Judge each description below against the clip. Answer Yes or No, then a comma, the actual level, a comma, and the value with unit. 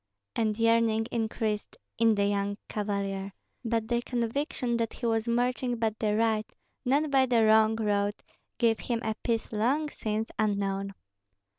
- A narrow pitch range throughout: Yes, narrow, 2.0 semitones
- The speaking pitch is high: Yes, high, 225 Hz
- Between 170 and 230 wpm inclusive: No, average, 150 wpm